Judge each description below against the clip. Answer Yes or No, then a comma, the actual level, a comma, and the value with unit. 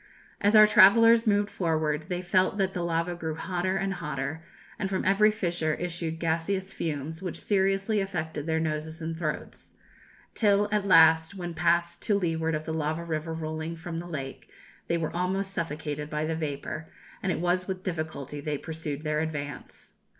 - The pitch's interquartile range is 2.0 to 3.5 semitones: Yes, average, 3.2 semitones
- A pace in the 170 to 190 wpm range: Yes, average, 175 wpm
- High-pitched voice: No, medium, 165 Hz